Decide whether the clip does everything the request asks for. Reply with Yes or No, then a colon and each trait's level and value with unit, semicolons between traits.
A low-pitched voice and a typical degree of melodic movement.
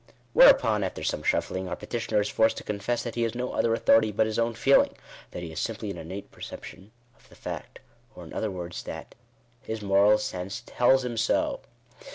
Yes: low, 110 Hz; average, 3.1 semitones